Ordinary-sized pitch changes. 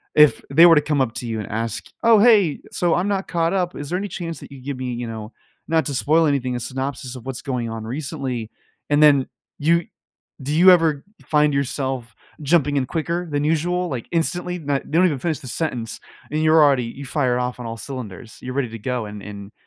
Yes: average, 4.8 semitones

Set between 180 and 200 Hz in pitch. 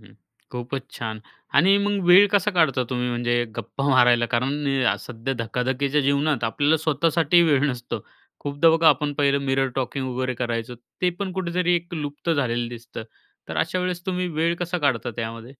No: medium, 140 Hz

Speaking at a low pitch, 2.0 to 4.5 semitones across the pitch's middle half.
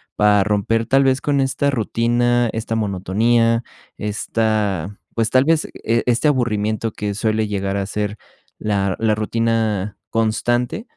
Yes: low, 110 Hz; narrow, 2.5 semitones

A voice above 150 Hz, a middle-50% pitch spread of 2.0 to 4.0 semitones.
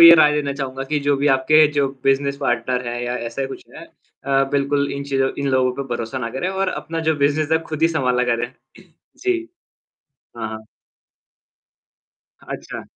No: medium, 140 Hz; narrow, 2.6 semitones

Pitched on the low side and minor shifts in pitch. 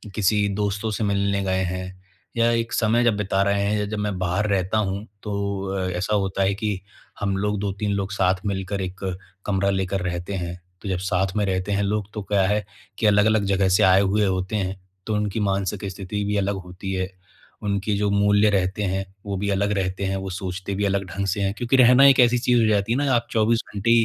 Yes: low, 100 Hz; narrow, 1.5 semitones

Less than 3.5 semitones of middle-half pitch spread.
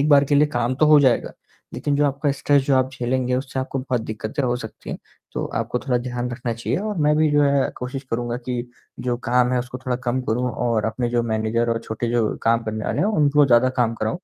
Yes: average, 2.8 semitones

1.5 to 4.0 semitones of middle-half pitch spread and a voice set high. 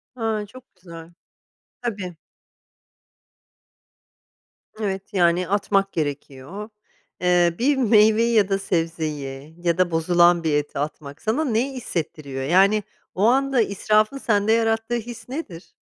No: average, 5.1 semitones; high, 195 Hz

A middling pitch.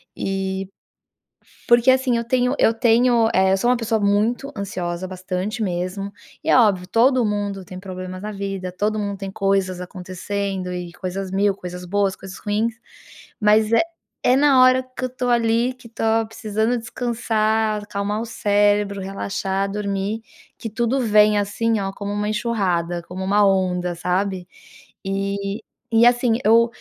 No: high, 205 Hz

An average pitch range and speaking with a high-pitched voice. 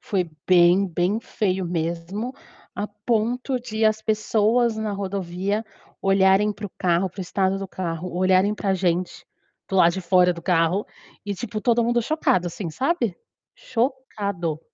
Yes: average, 3.3 semitones; high, 195 Hz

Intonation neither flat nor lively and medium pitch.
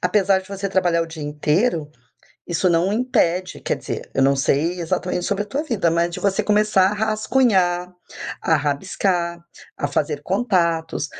Yes: average, 3.5 semitones; medium, 180 Hz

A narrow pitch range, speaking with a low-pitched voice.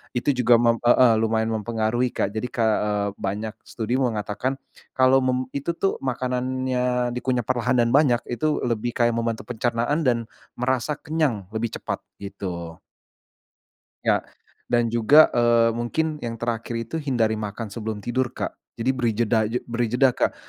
Yes: narrow, 2.2 semitones; low, 120 Hz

